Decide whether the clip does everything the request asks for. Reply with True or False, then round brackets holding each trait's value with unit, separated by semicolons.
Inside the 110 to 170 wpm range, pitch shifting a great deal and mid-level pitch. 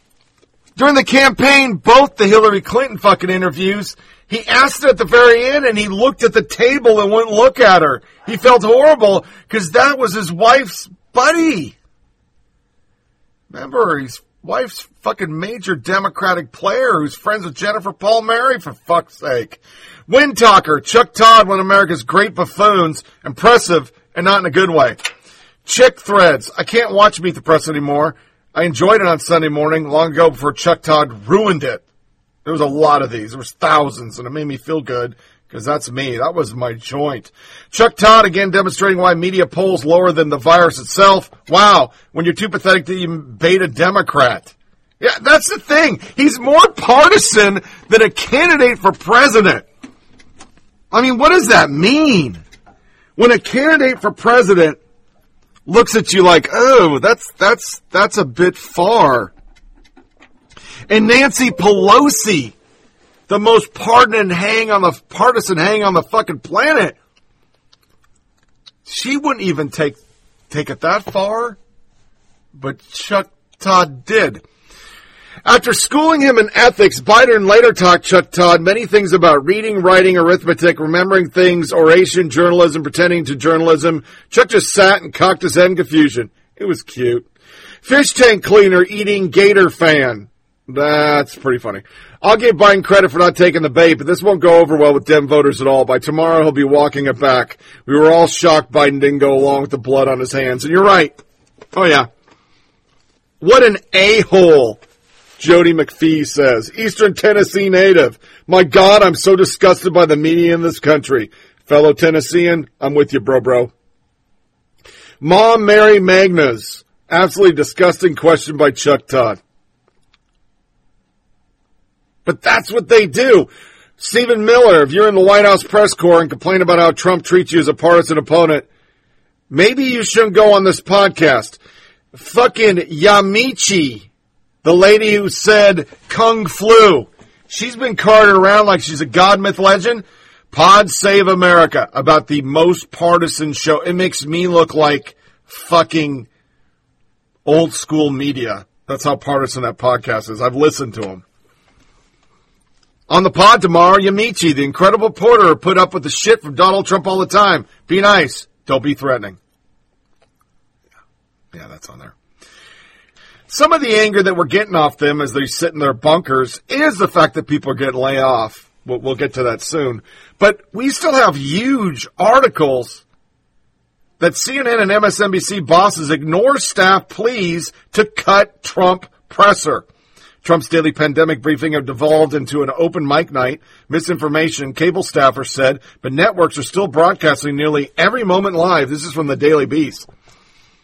True (160 wpm; 5.7 semitones; 180 Hz)